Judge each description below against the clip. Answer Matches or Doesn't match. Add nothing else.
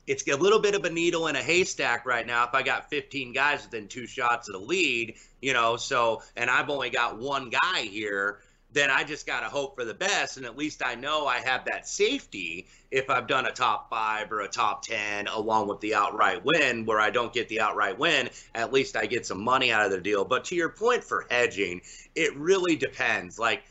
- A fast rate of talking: Matches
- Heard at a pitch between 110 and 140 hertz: Matches